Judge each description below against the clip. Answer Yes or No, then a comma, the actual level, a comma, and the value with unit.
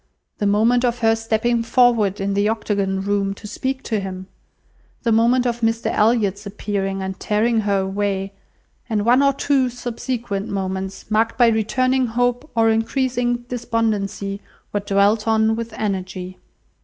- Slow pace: No, average, 150 wpm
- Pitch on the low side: No, high, 220 Hz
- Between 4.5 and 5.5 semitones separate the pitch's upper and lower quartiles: No, average, 3.2 semitones